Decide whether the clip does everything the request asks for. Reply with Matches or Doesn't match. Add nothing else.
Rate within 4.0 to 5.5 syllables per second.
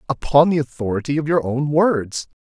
Matches